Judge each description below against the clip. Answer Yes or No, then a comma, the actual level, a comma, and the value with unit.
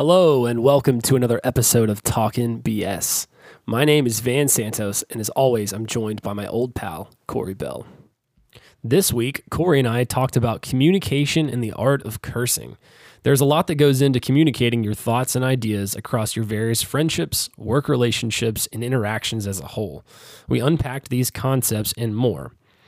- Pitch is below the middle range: Yes, low, 120 Hz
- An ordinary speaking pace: Yes, average, 175 wpm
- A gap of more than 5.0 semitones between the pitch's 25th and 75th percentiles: No, average, 3.5 semitones